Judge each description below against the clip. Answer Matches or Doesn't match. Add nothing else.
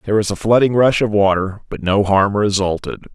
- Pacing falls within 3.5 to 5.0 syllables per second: Doesn't match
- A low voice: Matches